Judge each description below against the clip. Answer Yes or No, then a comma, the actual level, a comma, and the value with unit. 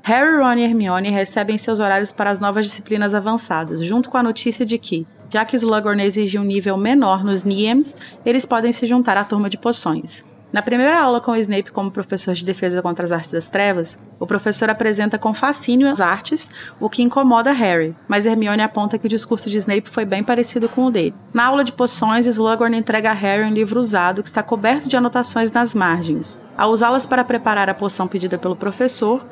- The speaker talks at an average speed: No, fast, 205 wpm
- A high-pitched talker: Yes, high, 220 Hz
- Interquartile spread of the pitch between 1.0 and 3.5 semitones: Yes, average, 3.1 semitones